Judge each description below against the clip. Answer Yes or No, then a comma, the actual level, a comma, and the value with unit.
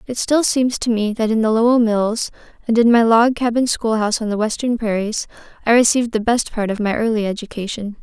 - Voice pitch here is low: No, high, 225 Hz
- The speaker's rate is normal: No, fast, 215 wpm